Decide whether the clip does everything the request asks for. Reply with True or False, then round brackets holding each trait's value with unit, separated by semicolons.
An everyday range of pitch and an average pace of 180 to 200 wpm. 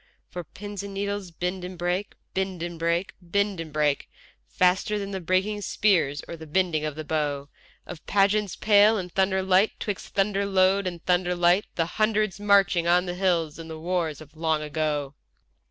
True (3.3 semitones; 185 wpm)